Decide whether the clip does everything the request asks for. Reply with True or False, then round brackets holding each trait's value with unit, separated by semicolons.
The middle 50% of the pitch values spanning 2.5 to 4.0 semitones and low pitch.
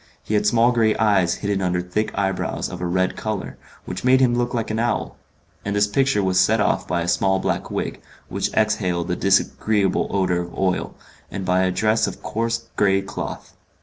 True (3.0 semitones; 100 Hz)